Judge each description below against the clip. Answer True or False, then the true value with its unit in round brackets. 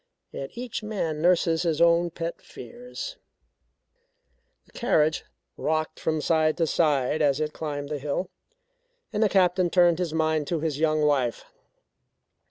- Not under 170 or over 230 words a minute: False (145 wpm)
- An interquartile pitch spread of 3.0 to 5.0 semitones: False (2.6 semitones)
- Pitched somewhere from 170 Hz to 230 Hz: False (160 Hz)